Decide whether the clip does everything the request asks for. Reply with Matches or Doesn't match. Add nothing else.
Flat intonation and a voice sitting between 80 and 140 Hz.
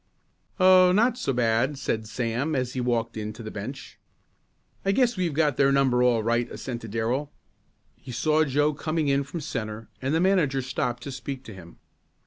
Doesn't match